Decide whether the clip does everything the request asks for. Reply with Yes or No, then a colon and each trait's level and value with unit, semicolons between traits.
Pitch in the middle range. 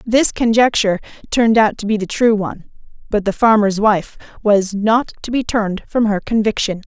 No: high, 215 Hz